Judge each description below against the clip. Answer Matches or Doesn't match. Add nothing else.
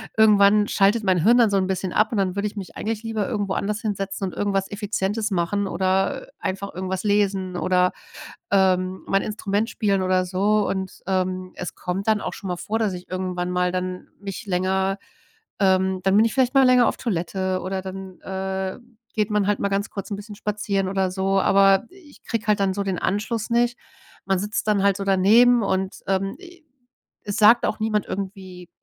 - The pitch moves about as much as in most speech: Doesn't match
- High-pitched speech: Matches